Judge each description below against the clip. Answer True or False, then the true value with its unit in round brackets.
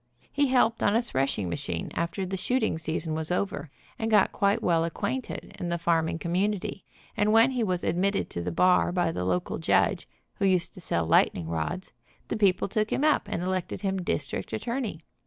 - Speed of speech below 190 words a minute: False (195 wpm)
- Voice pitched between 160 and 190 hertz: True (185 Hz)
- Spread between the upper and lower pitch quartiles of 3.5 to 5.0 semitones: True (4.5 semitones)